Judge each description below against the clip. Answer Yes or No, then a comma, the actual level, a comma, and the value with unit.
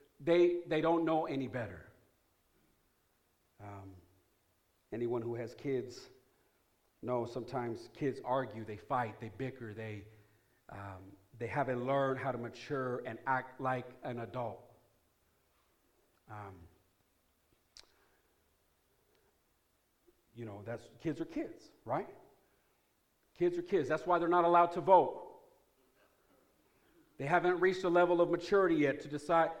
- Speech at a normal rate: No, slow, 120 wpm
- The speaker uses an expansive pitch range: Yes, wide, 6.3 semitones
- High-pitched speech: No, low, 130 Hz